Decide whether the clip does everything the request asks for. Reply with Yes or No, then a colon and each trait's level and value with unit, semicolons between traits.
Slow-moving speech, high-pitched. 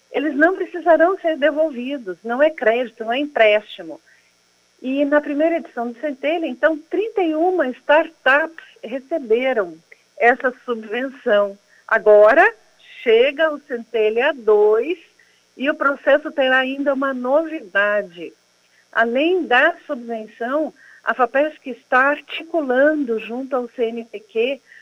Yes: slow, 110 wpm; very high, 275 Hz